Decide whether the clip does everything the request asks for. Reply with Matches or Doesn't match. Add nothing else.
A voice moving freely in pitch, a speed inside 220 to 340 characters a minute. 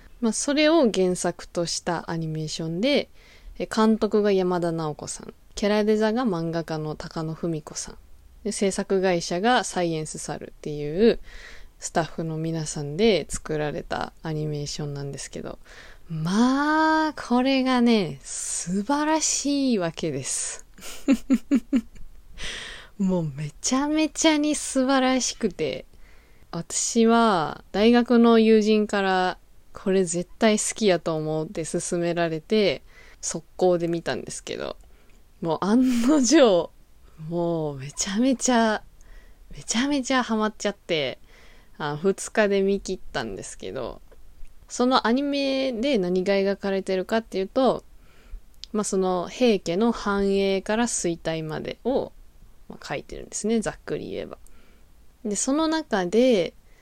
Matches